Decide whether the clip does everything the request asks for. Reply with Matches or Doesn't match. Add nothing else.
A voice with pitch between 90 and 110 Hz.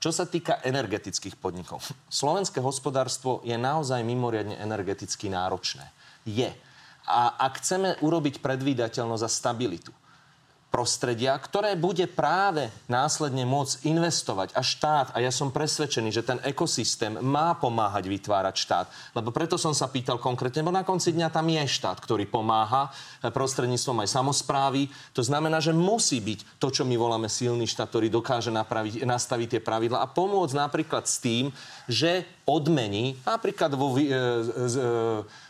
Doesn't match